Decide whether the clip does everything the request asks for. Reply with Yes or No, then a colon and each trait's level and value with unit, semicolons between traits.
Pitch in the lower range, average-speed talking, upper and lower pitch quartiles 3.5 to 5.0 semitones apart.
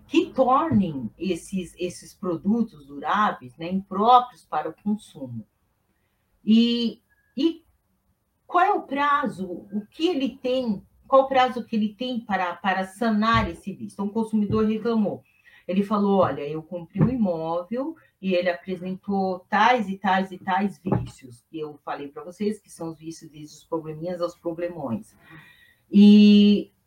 No: high, 195 Hz; average, 150 wpm; average, 4.7 semitones